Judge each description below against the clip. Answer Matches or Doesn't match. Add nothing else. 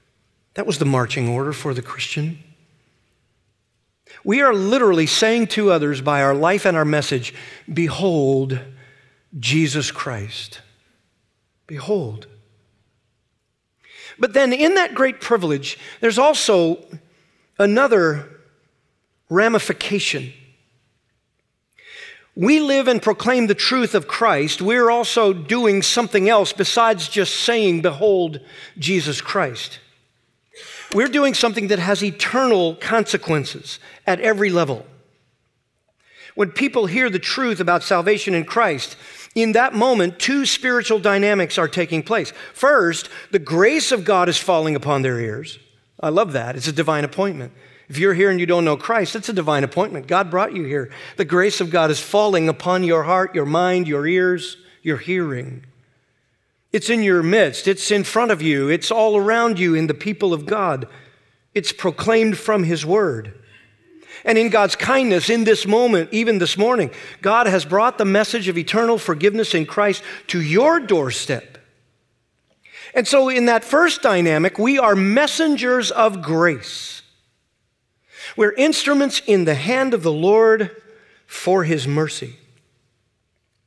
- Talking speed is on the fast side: Doesn't match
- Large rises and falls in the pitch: Matches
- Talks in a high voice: Doesn't match